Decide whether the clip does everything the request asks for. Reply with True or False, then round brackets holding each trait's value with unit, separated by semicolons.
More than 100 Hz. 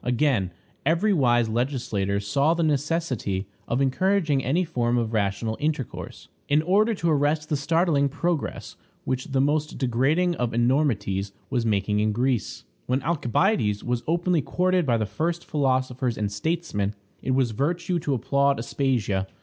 True (135 Hz)